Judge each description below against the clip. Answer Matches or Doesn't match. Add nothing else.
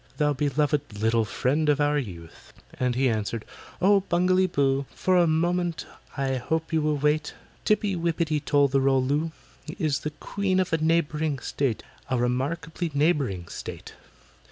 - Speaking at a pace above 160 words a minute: Doesn't match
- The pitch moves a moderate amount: Matches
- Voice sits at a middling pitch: Matches